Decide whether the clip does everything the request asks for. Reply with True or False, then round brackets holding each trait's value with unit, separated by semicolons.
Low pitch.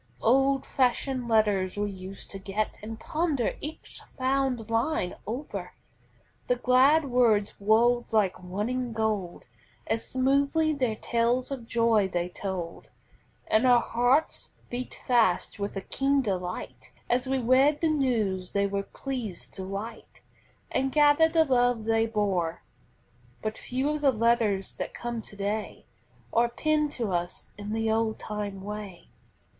False (230 Hz)